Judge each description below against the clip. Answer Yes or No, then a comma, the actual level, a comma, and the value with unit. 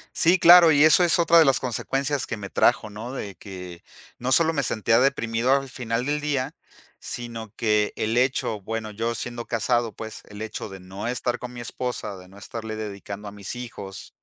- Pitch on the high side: No, low, 115 Hz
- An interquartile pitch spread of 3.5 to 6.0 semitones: Yes, average, 3.9 semitones